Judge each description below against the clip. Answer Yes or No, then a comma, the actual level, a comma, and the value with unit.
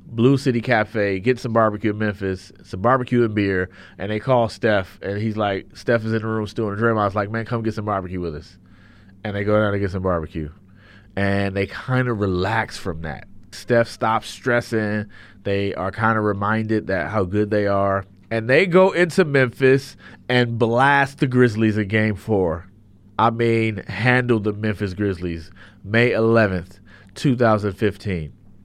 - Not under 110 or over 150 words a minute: No, average, 180 wpm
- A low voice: Yes, low, 105 Hz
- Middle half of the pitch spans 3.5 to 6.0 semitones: No, average, 2.7 semitones